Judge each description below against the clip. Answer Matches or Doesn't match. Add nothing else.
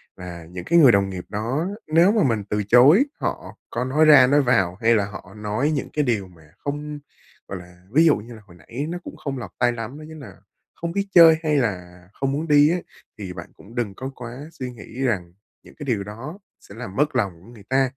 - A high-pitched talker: Doesn't match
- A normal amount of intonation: Doesn't match